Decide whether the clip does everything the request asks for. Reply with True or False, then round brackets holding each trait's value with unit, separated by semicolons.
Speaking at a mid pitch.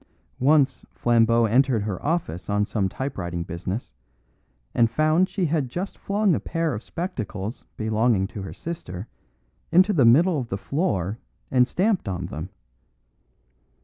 False (120 Hz)